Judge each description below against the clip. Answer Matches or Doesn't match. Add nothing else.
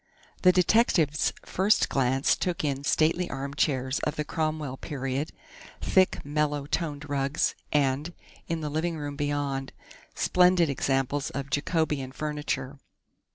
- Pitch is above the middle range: Doesn't match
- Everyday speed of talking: Doesn't match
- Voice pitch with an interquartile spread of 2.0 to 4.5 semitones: Matches